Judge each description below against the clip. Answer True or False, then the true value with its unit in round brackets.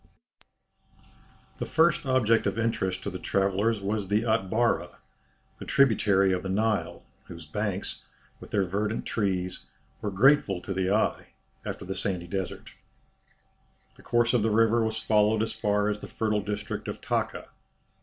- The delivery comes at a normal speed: True (155 wpm)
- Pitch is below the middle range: True (105 Hz)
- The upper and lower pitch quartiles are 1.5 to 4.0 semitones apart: True (2.7 semitones)